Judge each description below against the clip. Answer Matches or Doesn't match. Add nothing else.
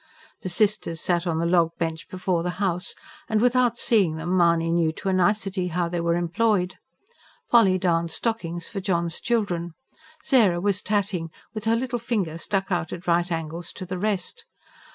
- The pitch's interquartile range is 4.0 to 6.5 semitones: Doesn't match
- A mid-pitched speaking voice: Matches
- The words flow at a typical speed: Matches